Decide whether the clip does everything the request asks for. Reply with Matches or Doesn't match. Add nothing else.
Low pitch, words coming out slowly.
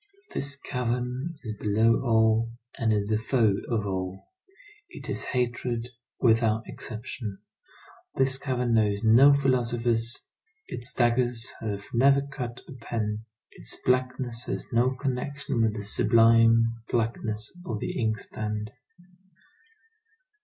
Matches